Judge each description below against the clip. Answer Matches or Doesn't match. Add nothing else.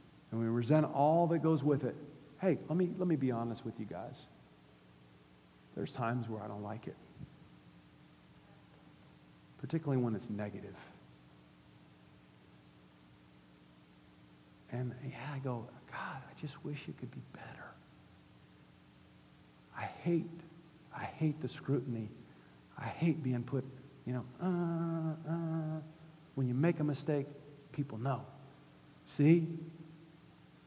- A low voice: Matches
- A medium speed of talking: Doesn't match